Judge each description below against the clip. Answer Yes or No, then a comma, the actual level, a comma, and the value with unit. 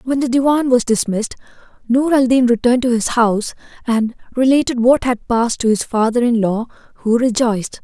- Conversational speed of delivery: Yes, average, 185 wpm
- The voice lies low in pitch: No, high, 240 Hz